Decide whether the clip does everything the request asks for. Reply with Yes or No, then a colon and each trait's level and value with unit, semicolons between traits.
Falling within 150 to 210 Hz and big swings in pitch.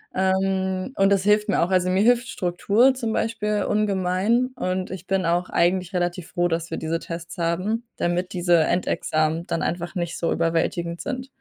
No: medium, 185 Hz; average, 3.1 semitones